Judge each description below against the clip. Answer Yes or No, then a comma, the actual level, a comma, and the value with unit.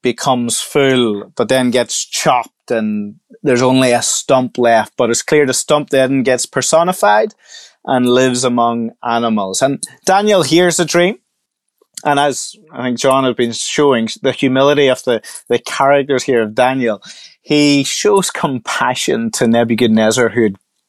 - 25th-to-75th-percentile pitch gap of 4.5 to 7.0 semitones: No, average, 3.5 semitones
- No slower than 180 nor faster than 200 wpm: No, average, 150 wpm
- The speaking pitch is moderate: No, low, 130 Hz